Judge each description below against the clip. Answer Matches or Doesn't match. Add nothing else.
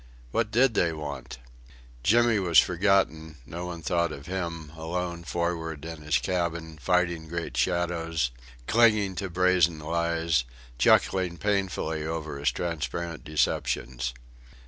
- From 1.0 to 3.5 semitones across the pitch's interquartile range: Matches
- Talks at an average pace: Doesn't match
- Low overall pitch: Matches